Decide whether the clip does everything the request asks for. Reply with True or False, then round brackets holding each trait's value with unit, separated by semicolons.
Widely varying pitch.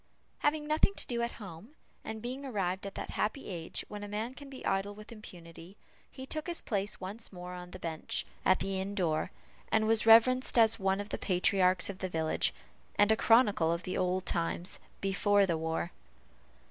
False (3.8 semitones)